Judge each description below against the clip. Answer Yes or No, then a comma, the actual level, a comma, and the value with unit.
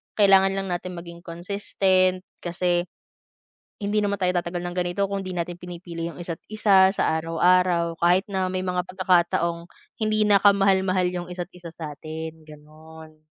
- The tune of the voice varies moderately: No, narrow, 2.0 semitones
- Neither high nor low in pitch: Yes, medium, 180 Hz